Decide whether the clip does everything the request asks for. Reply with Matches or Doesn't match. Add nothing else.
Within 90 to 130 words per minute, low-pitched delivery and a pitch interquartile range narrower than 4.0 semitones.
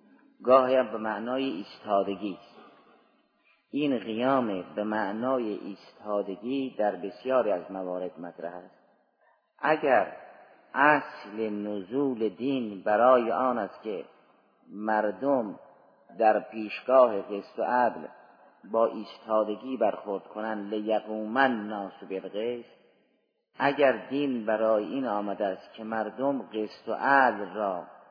Matches